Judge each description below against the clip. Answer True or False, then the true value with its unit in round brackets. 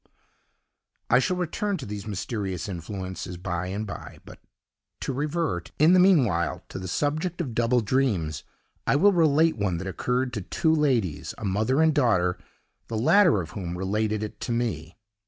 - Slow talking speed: False (170 wpm)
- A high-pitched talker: False (110 Hz)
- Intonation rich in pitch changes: True (7.9 semitones)